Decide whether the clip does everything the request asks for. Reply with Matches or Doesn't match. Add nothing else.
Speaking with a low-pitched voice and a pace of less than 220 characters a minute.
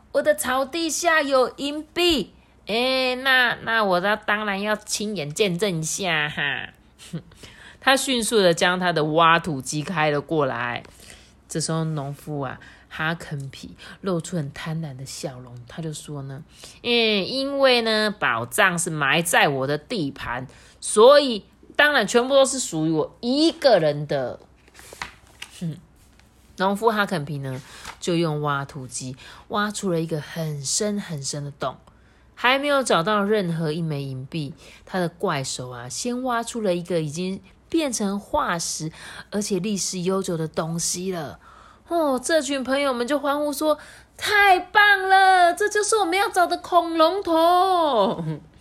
Doesn't match